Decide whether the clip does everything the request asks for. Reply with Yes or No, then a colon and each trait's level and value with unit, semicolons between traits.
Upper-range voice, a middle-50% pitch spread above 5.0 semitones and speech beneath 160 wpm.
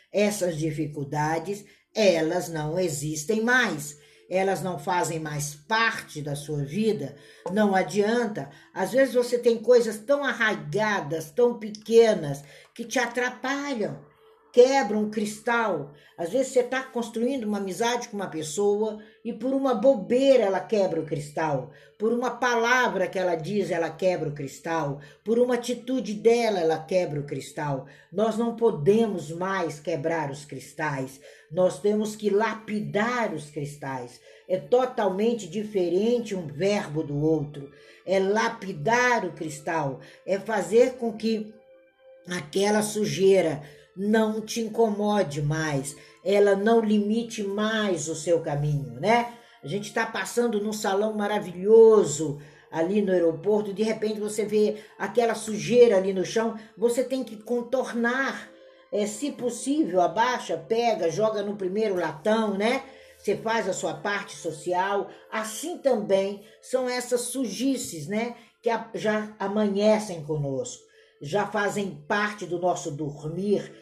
Yes: high, 205 Hz; wide, 5.5 semitones; average, 135 wpm